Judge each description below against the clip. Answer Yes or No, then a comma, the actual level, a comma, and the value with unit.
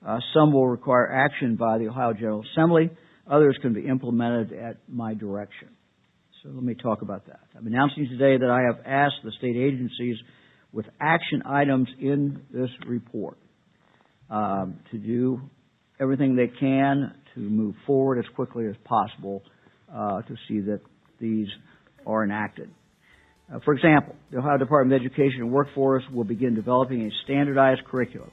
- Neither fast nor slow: Yes, average, 160 wpm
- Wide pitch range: No, average, 3.5 semitones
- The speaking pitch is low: Yes, low, 125 Hz